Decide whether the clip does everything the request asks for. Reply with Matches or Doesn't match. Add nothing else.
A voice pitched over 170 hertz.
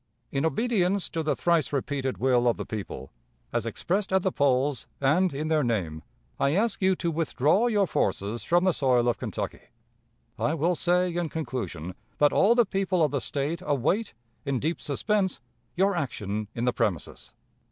Doesn't match